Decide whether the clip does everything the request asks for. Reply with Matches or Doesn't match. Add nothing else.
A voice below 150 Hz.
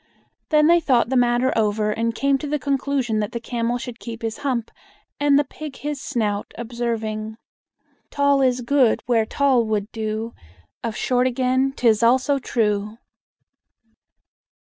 Doesn't match